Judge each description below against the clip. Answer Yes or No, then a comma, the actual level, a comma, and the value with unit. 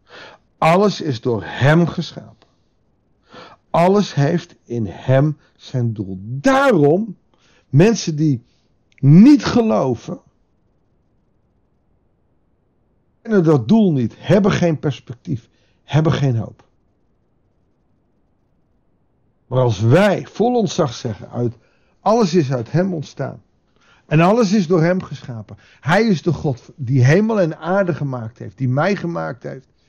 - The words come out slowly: Yes, slow, 120 wpm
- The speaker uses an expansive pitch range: Yes, wide, 6.6 semitones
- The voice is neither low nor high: Yes, medium, 155 Hz